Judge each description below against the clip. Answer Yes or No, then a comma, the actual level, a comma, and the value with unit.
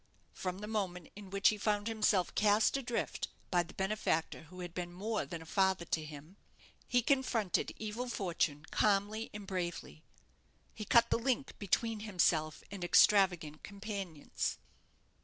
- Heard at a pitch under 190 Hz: No, high, 195 Hz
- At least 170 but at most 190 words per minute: No, average, 150 wpm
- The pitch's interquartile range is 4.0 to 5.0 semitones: No, average, 3.6 semitones